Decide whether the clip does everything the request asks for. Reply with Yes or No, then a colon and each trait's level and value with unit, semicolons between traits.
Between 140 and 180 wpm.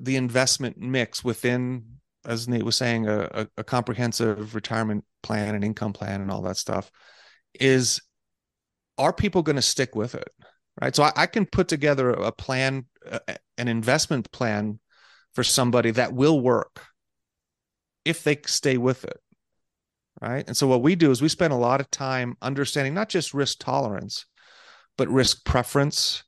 Yes: average, 165 wpm